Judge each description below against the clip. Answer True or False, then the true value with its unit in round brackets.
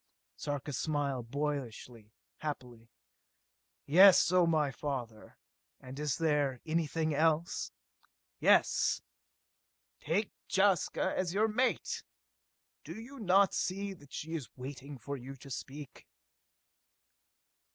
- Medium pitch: True (150 Hz)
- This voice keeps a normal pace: False (105 wpm)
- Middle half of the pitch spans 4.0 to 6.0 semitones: True (4.3 semitones)